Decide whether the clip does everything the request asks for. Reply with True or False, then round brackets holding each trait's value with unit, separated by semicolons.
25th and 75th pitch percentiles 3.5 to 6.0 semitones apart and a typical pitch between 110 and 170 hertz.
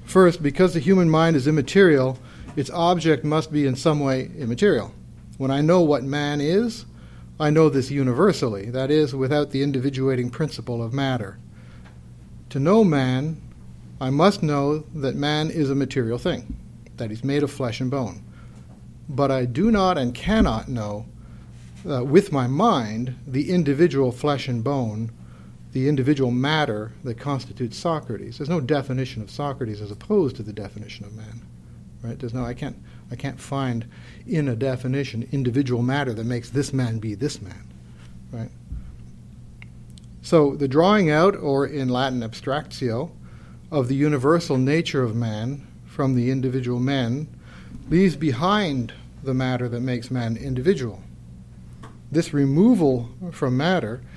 True (4.1 semitones; 135 Hz)